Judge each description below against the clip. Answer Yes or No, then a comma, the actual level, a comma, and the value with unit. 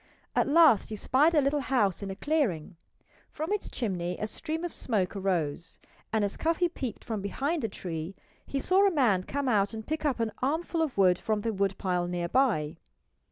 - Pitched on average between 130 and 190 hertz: No, high, 220 Hz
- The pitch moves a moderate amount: No, wide, 7.5 semitones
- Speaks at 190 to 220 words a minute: Yes, average, 195 wpm